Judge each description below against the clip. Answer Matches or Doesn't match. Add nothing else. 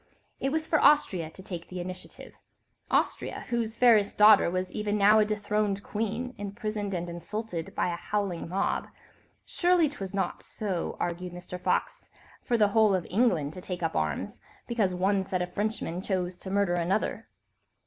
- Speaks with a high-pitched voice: Matches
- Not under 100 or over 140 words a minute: Doesn't match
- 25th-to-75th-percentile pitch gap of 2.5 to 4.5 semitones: Matches